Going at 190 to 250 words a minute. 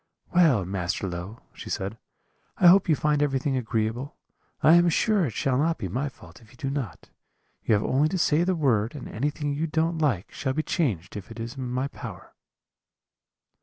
Yes: average, 200 wpm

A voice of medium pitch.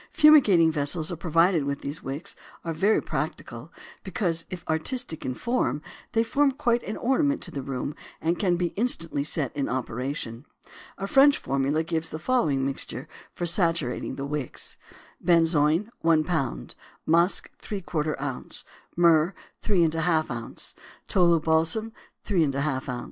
Yes: medium, 165 Hz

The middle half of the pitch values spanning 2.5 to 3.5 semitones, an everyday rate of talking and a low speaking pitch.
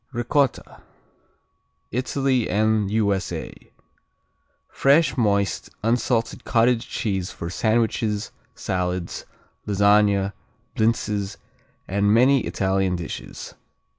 No: average, 3.2 semitones; slow, 75 wpm; low, 105 Hz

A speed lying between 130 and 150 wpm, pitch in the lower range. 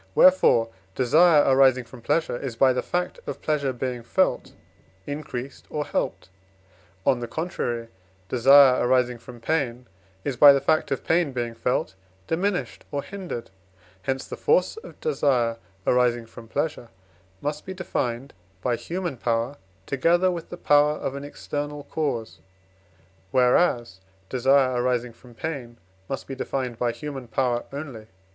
Yes: average, 145 wpm; low, 130 Hz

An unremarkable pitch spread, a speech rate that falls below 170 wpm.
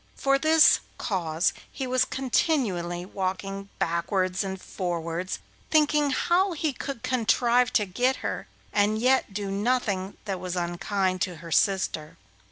No: wide, 5.8 semitones; slow, 135 wpm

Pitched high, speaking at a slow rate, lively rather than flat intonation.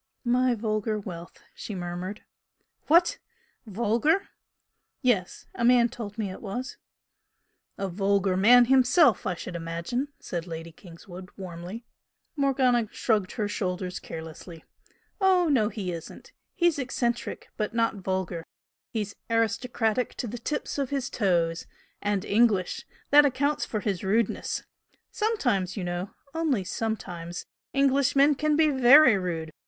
Yes: high, 215 Hz; slow, 130 wpm; wide, 5.7 semitones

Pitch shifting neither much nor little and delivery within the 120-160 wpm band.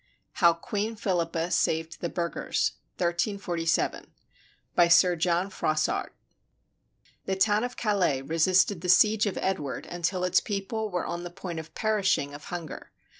Yes: average, 3.1 semitones; slow, 135 wpm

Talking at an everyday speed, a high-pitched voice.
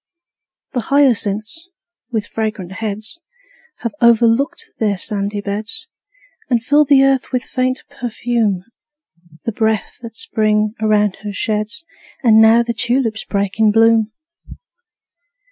No: slow, 120 wpm; high, 220 Hz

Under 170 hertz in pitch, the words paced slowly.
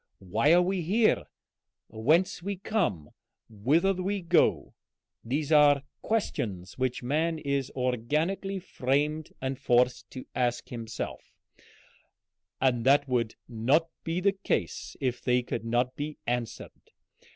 Yes: low, 135 Hz; slow, 125 wpm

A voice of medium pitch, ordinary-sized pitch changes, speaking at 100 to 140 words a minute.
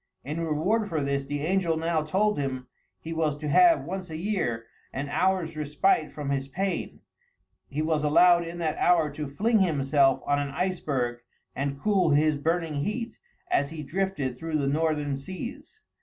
No: medium, 155 Hz; average, 4.2 semitones; average, 170 wpm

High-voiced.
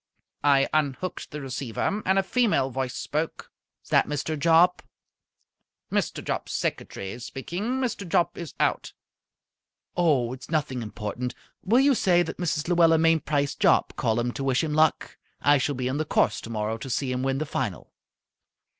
No: medium, 145 Hz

